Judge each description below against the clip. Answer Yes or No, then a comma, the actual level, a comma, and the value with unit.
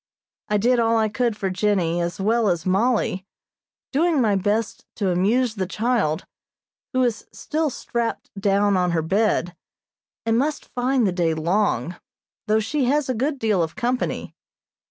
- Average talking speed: Yes, average, 160 wpm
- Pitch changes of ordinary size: Yes, average, 4.8 semitones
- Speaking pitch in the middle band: No, high, 215 Hz